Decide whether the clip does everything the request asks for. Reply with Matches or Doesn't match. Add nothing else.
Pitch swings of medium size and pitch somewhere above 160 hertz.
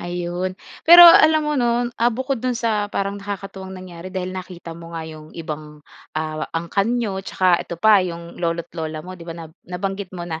Matches